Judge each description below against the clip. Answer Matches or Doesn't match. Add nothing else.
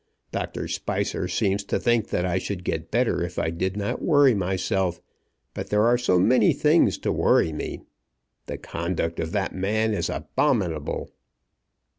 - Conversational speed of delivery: Matches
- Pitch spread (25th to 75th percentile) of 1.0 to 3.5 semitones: Doesn't match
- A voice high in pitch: Doesn't match